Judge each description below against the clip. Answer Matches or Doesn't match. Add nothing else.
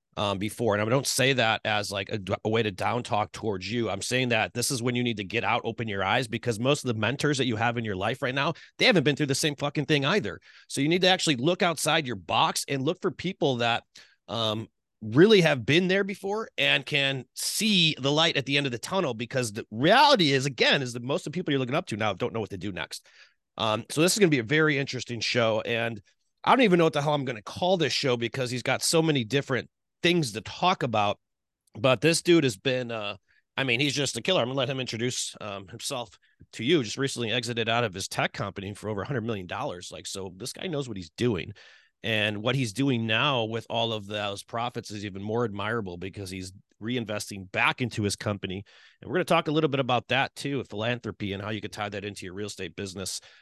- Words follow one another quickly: Matches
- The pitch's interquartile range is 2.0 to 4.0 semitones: Doesn't match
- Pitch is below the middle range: Matches